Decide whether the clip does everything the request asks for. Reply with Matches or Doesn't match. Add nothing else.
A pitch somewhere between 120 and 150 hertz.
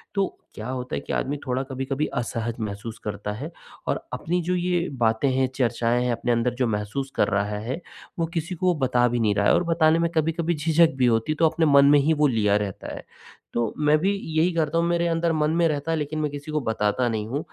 Matches